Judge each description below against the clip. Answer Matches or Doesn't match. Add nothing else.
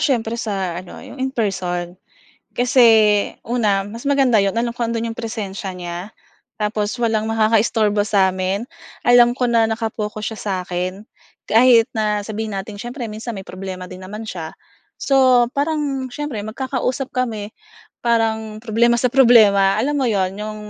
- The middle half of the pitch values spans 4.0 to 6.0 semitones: Doesn't match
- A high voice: Matches